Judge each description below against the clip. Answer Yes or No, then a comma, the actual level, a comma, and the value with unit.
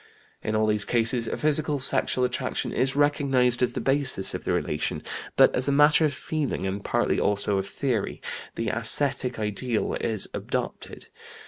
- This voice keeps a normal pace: Yes, average, 165 wpm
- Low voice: Yes, low, 125 Hz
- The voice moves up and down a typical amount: Yes, average, 4.4 semitones